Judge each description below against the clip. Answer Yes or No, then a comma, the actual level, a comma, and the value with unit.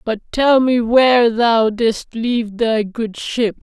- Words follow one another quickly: No, average, 160 wpm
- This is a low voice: No, high, 230 Hz